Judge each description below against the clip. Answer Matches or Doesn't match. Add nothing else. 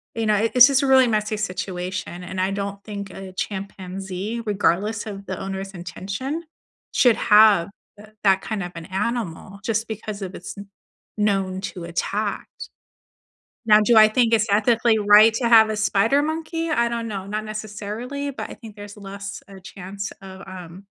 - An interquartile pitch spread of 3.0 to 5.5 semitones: Doesn't match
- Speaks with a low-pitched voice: Doesn't match